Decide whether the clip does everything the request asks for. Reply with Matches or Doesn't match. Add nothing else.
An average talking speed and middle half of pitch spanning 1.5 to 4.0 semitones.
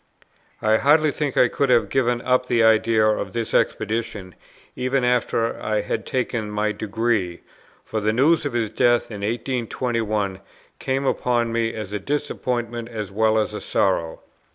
Matches